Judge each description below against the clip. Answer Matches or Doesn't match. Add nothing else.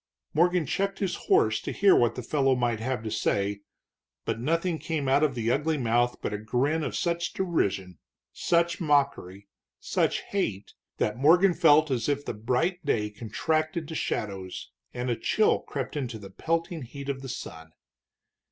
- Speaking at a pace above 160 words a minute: Matches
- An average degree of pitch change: Doesn't match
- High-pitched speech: Doesn't match